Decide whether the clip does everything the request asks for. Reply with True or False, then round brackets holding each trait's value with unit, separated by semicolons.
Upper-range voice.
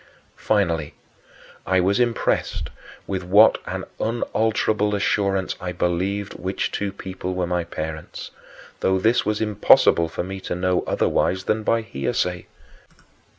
False (95 Hz)